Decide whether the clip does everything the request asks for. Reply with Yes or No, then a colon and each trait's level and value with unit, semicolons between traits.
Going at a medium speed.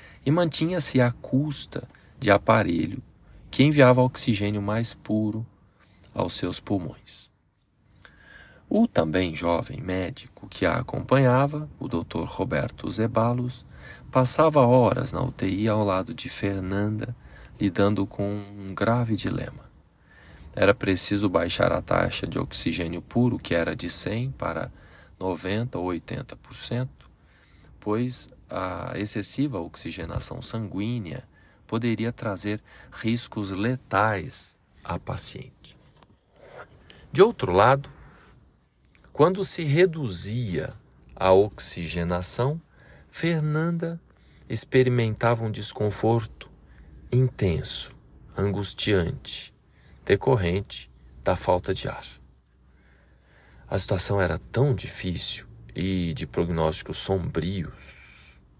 No: slow, 95 wpm